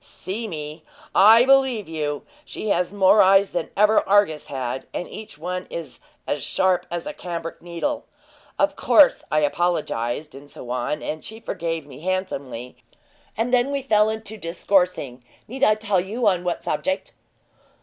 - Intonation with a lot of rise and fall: Yes, wide, 5.9 semitones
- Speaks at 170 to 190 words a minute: No, average, 160 wpm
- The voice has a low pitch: No, medium, 180 Hz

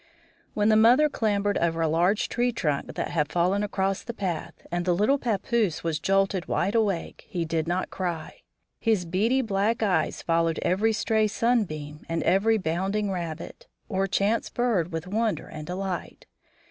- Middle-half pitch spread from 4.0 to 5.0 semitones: Yes, average, 4.3 semitones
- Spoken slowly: No, average, 165 wpm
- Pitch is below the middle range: No, high, 195 Hz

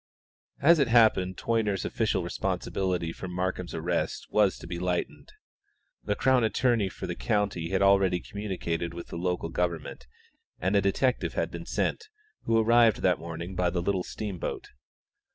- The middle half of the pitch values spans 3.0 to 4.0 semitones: Yes, average, 3.5 semitones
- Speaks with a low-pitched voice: Yes, very low, 95 Hz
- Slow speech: No, average, 155 wpm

